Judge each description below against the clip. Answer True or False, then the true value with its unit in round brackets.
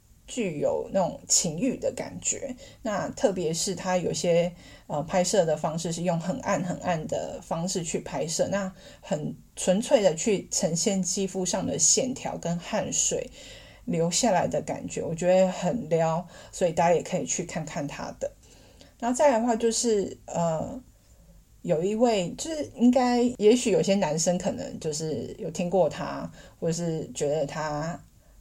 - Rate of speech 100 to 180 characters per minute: False (230 characters per minute)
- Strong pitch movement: False (4.8 semitones)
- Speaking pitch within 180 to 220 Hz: True (185 Hz)